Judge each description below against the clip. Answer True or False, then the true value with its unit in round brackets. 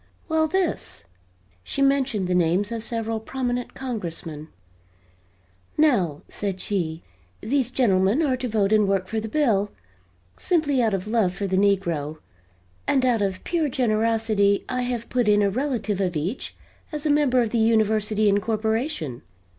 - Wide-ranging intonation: False (4.4 semitones)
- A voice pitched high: True (220 Hz)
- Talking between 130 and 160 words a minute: True (155 wpm)